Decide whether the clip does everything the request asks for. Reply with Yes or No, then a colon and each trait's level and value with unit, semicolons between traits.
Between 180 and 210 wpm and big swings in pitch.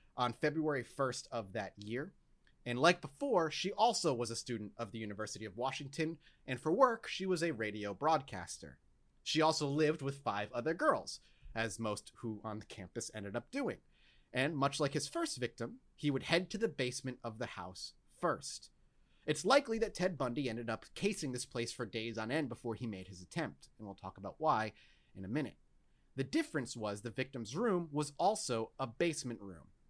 Yes: average, 195 wpm; wide, 6.1 semitones